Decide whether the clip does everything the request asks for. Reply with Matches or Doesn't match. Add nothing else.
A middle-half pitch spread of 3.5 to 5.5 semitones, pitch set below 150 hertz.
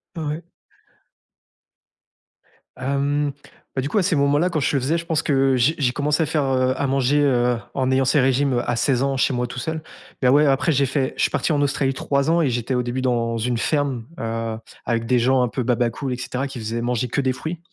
Doesn't match